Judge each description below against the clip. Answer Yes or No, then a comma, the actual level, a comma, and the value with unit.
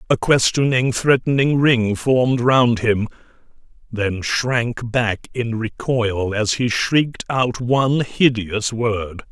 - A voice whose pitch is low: Yes, low, 120 Hz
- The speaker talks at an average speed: No, slow, 120 wpm